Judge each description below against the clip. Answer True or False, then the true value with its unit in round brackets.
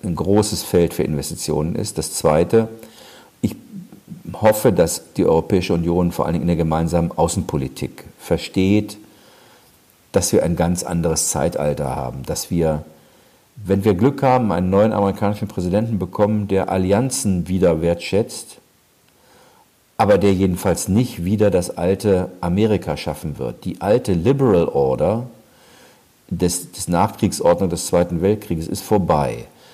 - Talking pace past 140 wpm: False (130 wpm)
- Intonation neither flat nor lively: True (3.7 semitones)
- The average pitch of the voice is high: False (95 Hz)